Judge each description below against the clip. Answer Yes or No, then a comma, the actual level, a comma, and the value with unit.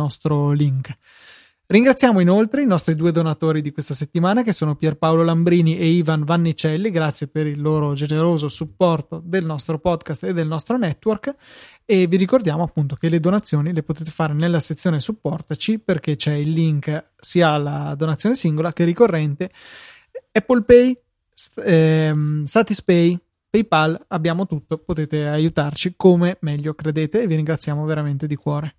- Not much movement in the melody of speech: No, average, 3.1 semitones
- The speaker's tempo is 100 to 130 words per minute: No, average, 150 wpm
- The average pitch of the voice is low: No, medium, 160 Hz